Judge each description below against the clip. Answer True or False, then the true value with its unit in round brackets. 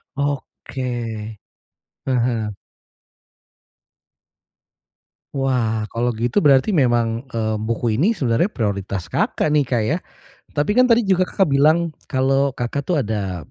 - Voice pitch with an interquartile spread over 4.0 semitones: True (4.5 semitones)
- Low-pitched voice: True (125 Hz)